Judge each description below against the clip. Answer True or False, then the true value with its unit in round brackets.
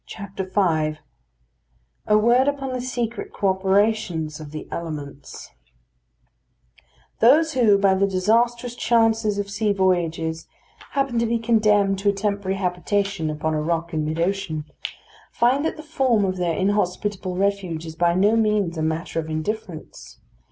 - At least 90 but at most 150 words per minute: True (145 wpm)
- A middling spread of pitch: True (5.0 semitones)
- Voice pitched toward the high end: True (195 Hz)